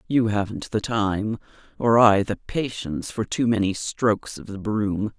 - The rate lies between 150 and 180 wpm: Yes, average, 175 wpm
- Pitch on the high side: No, low, 110 Hz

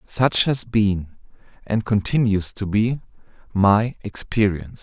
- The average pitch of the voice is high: No, low, 105 Hz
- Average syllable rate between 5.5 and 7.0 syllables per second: No, 3.8 syllables/s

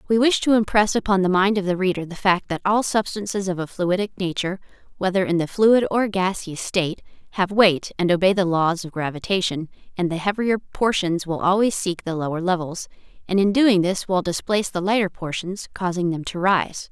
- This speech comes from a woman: Yes, female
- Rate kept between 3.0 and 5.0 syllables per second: No, 5.4 syllables/s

